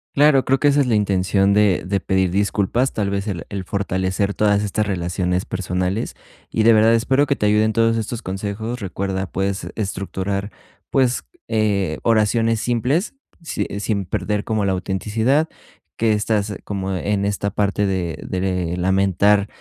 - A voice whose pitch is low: Yes, low, 100 Hz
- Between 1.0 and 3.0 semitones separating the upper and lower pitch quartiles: Yes, narrow, 2.6 semitones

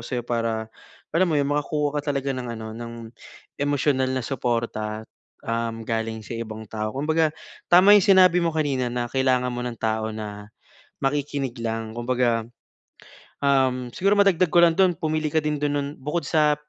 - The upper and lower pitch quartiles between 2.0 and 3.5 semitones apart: No, average, 4.7 semitones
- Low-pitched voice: Yes, low, 130 Hz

